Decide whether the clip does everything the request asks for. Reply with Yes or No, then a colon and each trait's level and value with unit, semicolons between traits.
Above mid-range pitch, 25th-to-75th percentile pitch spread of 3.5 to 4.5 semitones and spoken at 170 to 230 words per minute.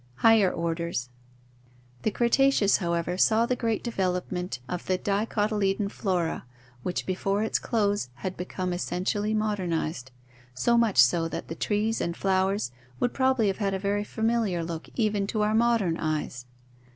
No: high, 195 Hz; average, 4.2 semitones; average, 155 wpm